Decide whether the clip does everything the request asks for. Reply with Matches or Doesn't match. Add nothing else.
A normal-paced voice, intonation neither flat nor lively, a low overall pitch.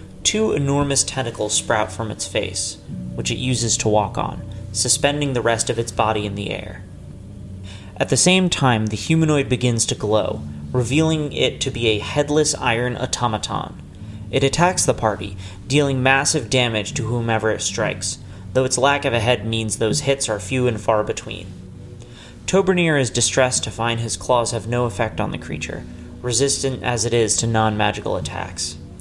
Matches